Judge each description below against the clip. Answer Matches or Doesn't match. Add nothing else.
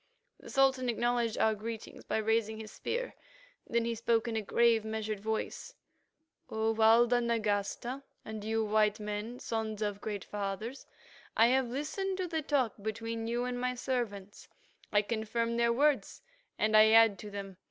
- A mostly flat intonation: Matches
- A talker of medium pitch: Doesn't match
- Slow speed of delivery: Doesn't match